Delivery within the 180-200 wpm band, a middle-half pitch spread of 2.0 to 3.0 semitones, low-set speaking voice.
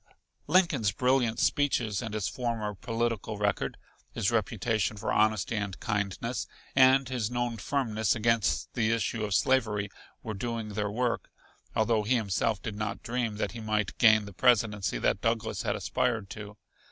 No: average, 155 wpm; narrow, 2.4 semitones; low, 110 Hz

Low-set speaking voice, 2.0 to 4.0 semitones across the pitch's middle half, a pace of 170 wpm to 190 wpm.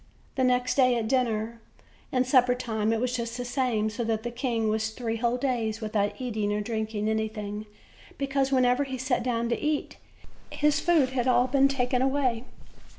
No: high, 245 Hz; average, 2.7 semitones; average, 185 wpm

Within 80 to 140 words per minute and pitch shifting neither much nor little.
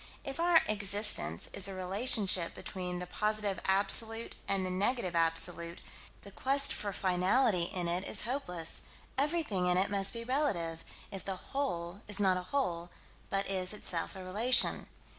No: average, 160 wpm; average, 3.8 semitones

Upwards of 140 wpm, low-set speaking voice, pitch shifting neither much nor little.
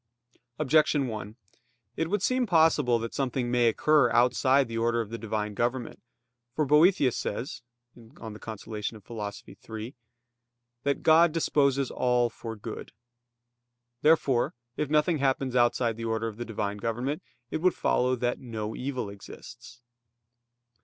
No: slow, 135 wpm; low, 120 Hz; average, 3.9 semitones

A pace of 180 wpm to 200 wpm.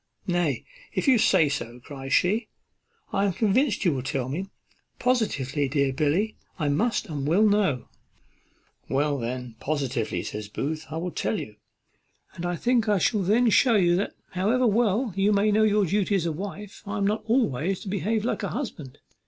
Yes: average, 185 wpm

